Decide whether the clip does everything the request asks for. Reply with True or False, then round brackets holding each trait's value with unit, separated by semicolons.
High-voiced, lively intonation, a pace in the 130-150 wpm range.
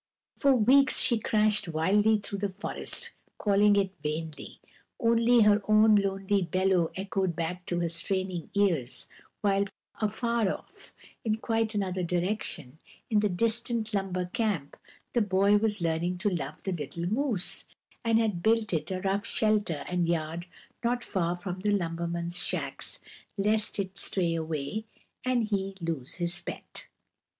False (195 Hz; 3.8 semitones; 145 wpm)